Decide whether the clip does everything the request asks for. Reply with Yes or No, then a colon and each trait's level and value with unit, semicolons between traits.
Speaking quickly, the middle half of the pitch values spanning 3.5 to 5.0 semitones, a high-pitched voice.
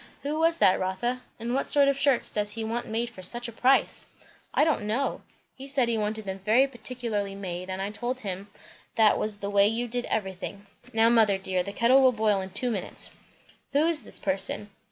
Yes: fast, 215 wpm; average, 3.9 semitones; high, 220 Hz